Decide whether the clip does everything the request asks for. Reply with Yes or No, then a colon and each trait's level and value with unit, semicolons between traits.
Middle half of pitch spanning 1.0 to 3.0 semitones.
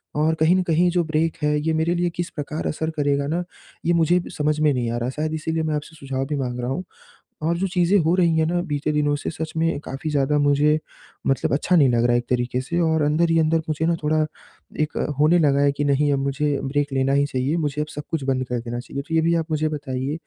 Yes: narrow, 2.6 semitones